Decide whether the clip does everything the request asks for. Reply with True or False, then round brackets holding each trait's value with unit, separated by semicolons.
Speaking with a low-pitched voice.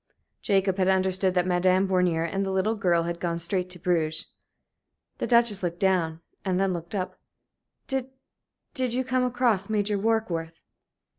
False (190 Hz)